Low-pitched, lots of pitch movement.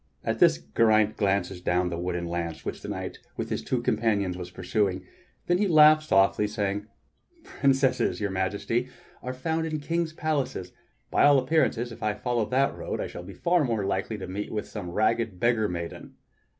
Yes: low, 105 Hz; wide, 5.9 semitones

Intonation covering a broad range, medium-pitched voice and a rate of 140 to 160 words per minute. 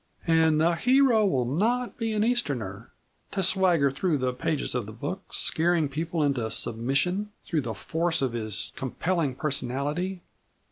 Yes: wide, 6.3 semitones; medium, 155 Hz; average, 150 wpm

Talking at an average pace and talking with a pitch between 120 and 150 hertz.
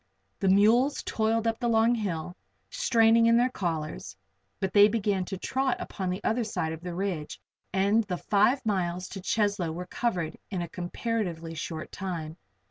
No: average, 170 wpm; high, 195 Hz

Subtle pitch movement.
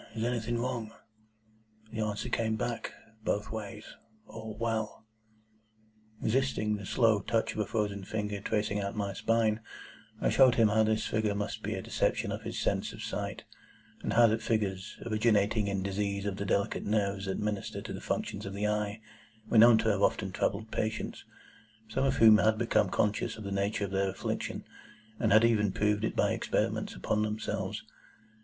Yes: narrow, 1.7 semitones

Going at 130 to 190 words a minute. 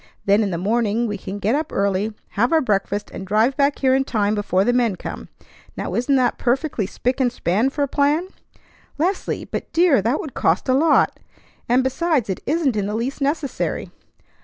No: average, 200 wpm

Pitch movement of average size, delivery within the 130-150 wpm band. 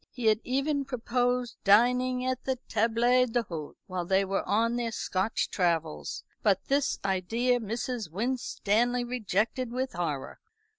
Yes: average, 4.2 semitones; slow, 135 wpm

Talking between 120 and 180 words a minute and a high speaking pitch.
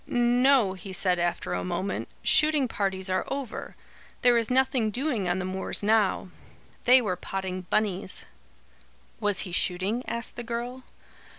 Yes: average, 150 wpm; high, 210 Hz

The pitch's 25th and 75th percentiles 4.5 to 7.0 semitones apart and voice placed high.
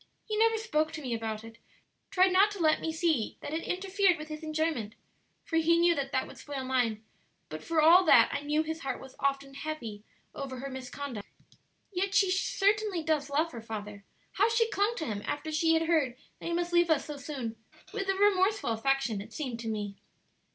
Yes: wide, 5.5 semitones; very high, 310 Hz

